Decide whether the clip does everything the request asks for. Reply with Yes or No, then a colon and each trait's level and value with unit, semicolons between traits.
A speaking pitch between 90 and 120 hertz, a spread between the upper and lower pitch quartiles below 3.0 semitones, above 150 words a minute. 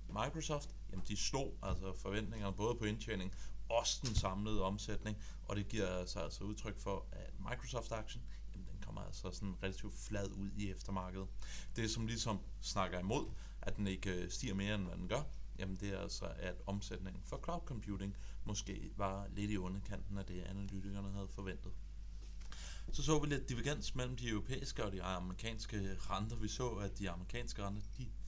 Yes: low, 100 Hz; narrow, 2.4 semitones; average, 175 wpm